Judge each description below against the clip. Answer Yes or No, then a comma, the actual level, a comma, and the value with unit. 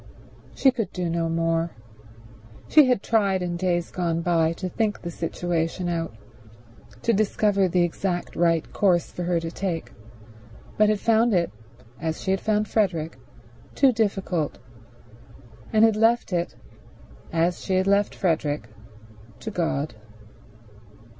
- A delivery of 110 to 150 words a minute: Yes, average, 140 wpm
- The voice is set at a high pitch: No, medium, 180 Hz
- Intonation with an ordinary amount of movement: Yes, average, 3.7 semitones